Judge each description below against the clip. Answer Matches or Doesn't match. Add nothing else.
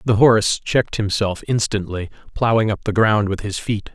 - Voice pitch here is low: Matches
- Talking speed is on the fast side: Doesn't match